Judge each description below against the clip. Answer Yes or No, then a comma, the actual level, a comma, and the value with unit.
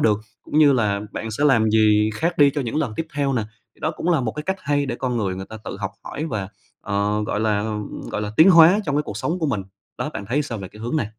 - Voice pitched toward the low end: Yes, low, 120 Hz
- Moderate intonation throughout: No, wide, 5.9 semitones